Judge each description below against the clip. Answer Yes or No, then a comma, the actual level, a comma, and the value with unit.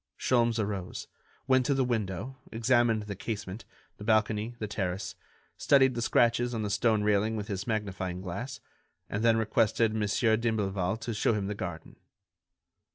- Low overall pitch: Yes, low, 110 Hz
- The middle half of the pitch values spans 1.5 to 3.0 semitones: Yes, narrow, 2.6 semitones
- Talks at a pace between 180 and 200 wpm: No, average, 160 wpm